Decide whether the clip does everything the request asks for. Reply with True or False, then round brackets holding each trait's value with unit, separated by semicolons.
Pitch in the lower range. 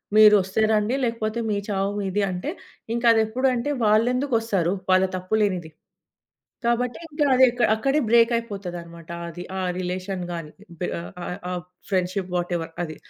False (205 Hz)